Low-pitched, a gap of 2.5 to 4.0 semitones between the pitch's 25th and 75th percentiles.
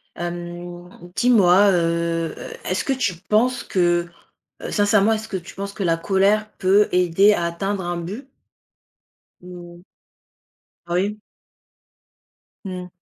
No: medium, 185 Hz; average, 2.9 semitones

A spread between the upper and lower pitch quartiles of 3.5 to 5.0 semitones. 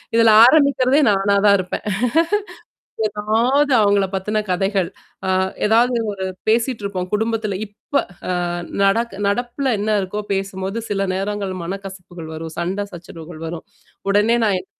No: average, 3.0 semitones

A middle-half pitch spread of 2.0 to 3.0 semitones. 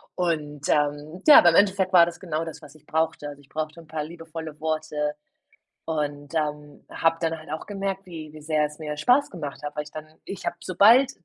Yes: narrow, 2.4 semitones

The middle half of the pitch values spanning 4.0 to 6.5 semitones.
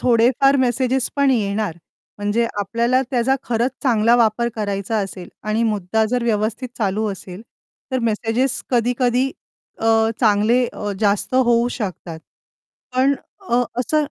No: average, 3.0 semitones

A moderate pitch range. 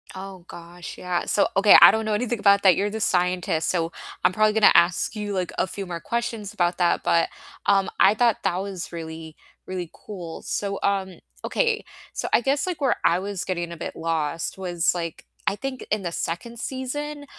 Yes: average, 3.7 semitones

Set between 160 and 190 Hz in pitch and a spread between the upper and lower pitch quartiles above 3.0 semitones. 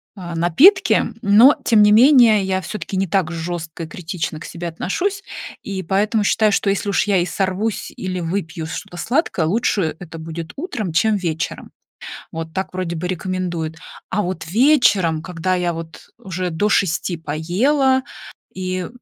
Yes: medium, 185 Hz; average, 4.0 semitones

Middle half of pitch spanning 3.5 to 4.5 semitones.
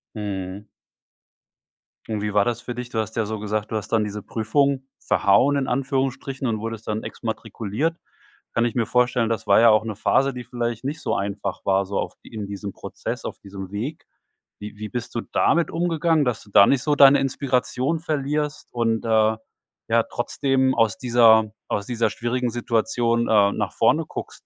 Yes: average, 3.8 semitones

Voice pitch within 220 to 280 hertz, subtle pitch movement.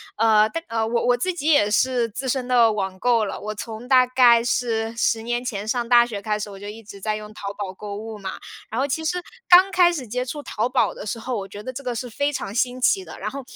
No: high, 230 Hz; average, 3.2 semitones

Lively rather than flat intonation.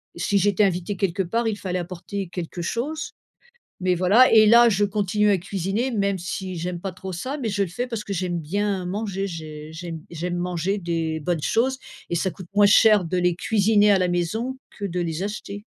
No: average, 2.9 semitones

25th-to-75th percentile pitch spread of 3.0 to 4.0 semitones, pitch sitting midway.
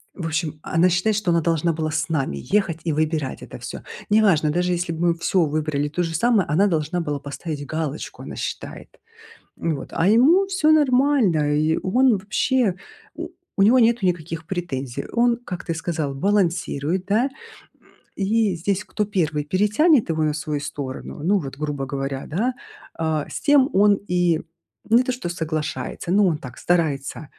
No: average, 5.2 semitones; medium, 170 Hz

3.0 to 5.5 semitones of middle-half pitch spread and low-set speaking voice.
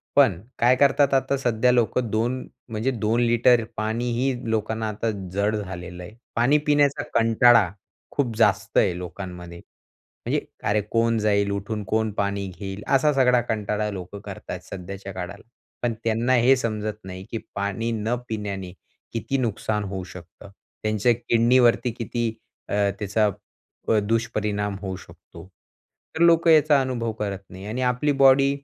Yes: average, 3.3 semitones; low, 110 Hz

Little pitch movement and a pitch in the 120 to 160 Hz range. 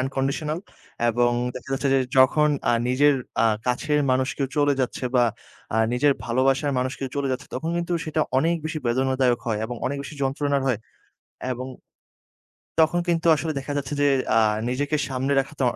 Yes: narrow, 2.3 semitones; low, 135 Hz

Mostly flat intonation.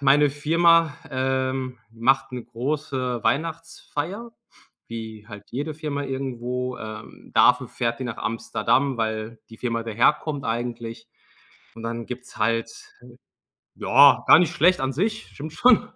No: average, 4.2 semitones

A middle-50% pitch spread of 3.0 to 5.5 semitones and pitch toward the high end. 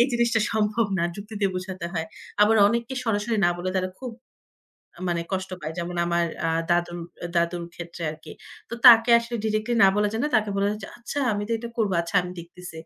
Yes: average, 4.6 semitones; high, 205 Hz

